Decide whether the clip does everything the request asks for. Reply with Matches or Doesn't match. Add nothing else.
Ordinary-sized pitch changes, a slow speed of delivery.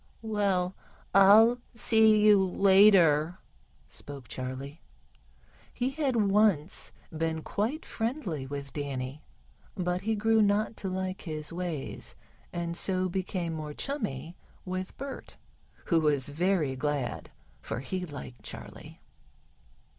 Doesn't match